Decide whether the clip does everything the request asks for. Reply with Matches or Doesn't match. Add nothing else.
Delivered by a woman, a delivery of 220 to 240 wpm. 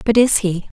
Matches